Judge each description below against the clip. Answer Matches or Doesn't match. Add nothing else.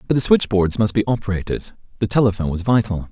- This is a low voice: Matches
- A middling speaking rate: Matches